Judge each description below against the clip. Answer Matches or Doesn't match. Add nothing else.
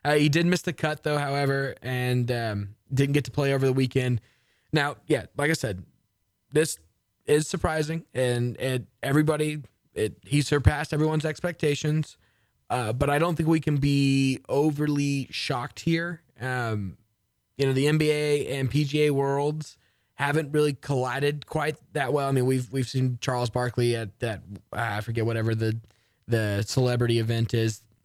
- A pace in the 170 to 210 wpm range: Doesn't match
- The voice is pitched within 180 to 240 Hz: Doesn't match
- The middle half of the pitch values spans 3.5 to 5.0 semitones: Matches